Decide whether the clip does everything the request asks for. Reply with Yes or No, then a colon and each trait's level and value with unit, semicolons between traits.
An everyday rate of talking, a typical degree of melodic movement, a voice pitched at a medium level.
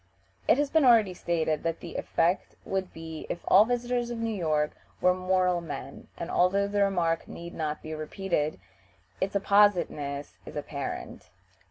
Yes: average, 160 wpm; average, 3.9 semitones; medium, 180 Hz